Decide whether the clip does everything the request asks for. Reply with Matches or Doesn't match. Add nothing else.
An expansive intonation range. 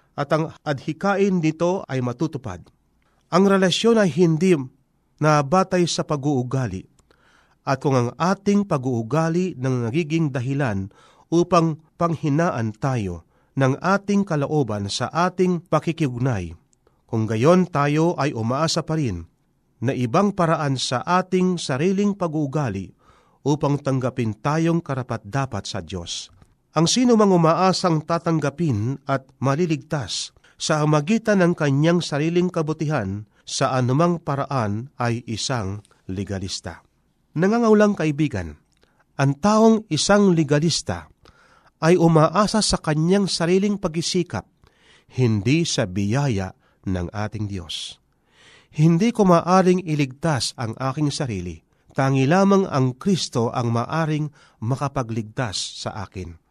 Matches